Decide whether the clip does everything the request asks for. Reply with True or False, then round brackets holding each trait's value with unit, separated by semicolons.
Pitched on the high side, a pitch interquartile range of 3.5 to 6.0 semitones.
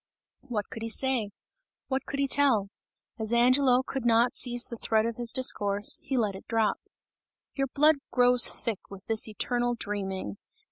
False (235 Hz; 3.1 semitones)